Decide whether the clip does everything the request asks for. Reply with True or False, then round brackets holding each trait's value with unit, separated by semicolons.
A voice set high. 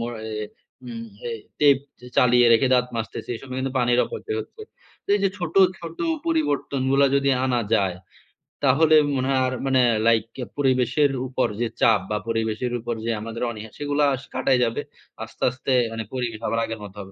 False (125 Hz)